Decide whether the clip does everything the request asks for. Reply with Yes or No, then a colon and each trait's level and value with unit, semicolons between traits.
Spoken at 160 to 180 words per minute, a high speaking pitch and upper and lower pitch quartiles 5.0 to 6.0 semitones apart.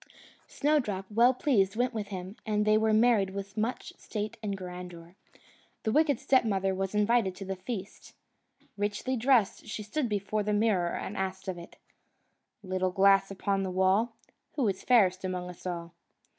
No: average, 165 wpm; high, 200 Hz; average, 2.9 semitones